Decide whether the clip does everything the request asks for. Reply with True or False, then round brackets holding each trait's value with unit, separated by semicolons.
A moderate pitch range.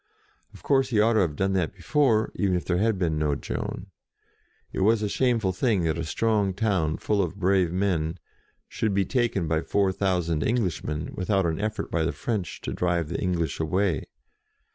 True (4.3 semitones)